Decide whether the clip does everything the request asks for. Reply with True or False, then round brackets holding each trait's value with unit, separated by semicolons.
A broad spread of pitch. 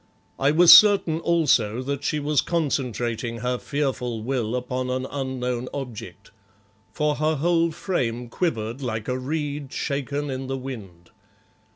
False (3.4 semitones)